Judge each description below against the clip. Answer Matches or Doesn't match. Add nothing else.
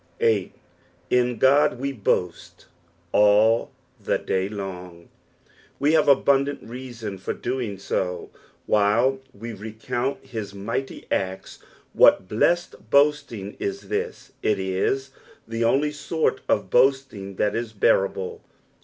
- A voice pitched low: Matches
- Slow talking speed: Matches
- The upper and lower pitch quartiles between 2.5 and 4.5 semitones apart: Doesn't match